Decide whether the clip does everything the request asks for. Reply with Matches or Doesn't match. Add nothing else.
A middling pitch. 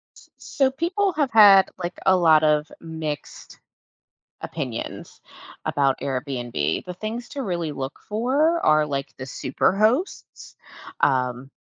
Matches